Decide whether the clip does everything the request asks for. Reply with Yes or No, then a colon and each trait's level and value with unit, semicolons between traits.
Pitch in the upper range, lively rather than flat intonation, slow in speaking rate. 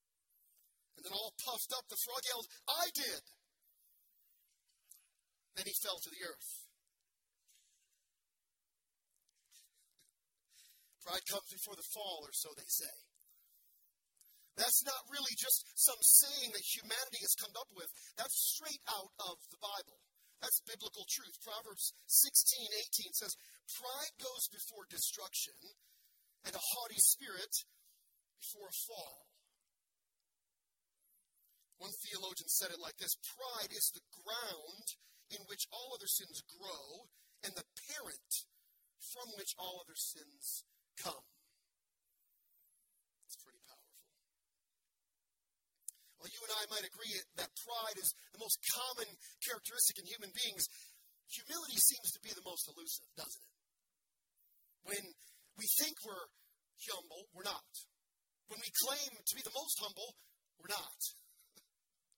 No: high, 230 Hz; average, 4.8 semitones; slow, 125 wpm